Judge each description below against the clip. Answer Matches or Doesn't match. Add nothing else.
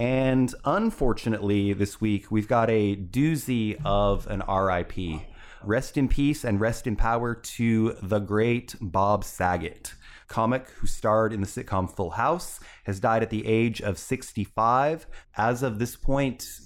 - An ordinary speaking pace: Matches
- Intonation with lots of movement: Doesn't match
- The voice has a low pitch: Matches